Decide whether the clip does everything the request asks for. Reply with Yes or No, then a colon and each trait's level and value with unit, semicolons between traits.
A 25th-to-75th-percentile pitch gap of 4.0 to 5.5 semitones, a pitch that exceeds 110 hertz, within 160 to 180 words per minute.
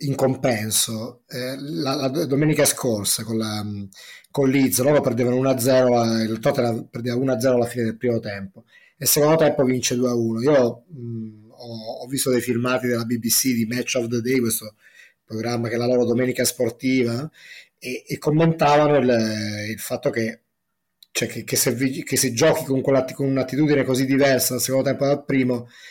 No: narrow, 2.5 semitones; low, 125 Hz; fast, 170 wpm